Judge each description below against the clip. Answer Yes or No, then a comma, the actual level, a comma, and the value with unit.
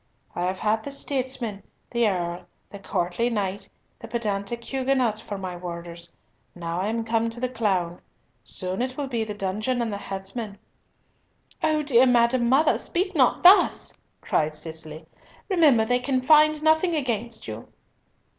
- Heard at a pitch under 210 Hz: No, high, 225 Hz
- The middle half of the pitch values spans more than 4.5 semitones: Yes, average, 5.3 semitones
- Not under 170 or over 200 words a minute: No, average, 155 wpm